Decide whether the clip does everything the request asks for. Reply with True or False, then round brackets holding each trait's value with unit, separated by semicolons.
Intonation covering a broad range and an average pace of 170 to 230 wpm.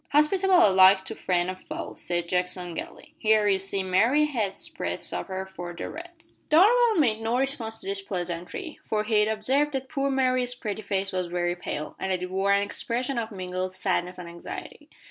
True (6.5 semitones; 190 wpm)